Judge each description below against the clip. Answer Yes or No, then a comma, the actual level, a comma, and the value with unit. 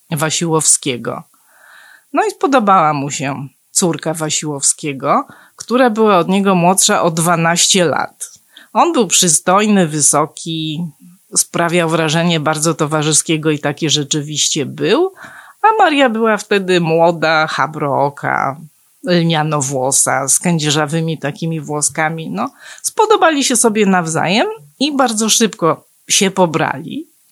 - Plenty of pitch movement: No, average, 4.7 semitones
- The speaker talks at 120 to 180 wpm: No, slow, 110 wpm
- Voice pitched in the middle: Yes, medium, 165 Hz